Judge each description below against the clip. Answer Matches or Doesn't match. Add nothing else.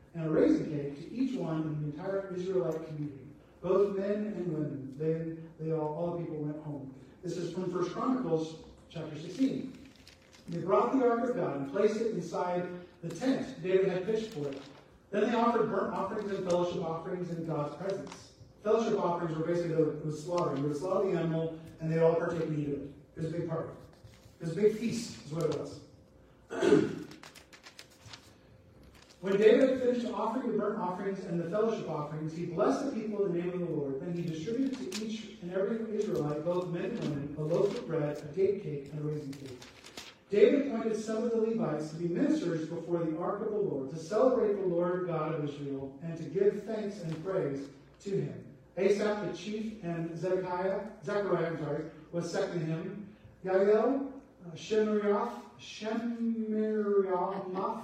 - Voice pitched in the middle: Matches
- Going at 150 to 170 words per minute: Doesn't match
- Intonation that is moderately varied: Matches